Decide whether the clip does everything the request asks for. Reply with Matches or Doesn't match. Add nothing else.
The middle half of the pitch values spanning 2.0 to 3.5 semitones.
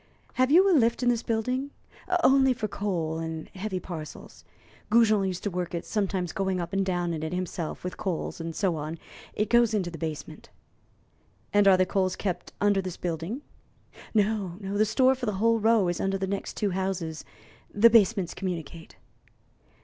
Doesn't match